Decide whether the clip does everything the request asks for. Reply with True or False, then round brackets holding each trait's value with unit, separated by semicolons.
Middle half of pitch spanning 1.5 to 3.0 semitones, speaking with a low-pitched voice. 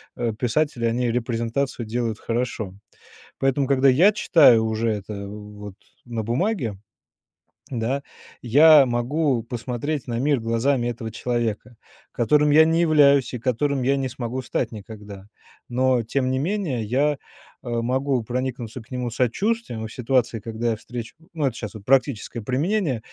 False (3.4 semitones; 125 Hz)